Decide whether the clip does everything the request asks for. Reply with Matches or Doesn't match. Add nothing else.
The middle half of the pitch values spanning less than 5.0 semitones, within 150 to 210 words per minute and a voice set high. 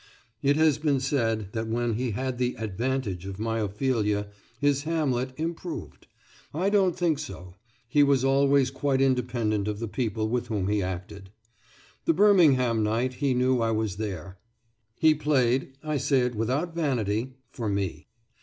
Doesn't match